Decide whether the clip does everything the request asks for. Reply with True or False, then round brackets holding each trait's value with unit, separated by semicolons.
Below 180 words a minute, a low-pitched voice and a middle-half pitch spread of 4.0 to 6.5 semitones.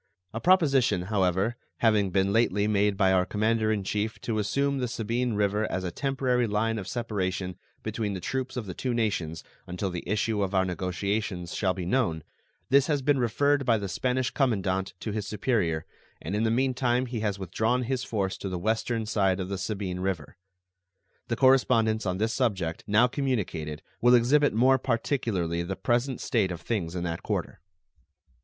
False (185 wpm; 110 Hz; 4.4 semitones)